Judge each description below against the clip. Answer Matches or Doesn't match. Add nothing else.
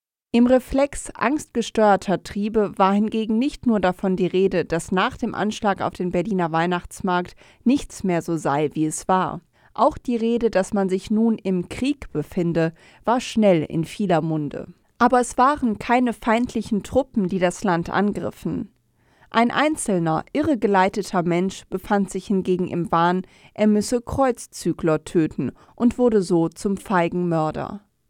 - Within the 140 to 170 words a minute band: Matches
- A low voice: Doesn't match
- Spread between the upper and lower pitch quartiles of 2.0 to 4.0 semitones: Doesn't match